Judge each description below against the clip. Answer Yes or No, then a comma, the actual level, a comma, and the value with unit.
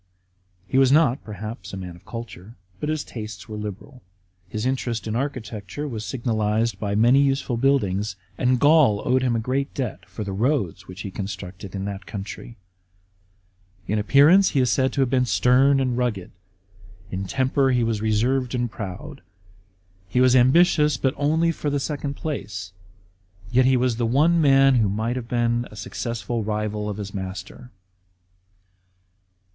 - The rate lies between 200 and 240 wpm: No, average, 165 wpm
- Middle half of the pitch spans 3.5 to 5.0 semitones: Yes, average, 4.3 semitones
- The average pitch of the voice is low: Yes, low, 120 Hz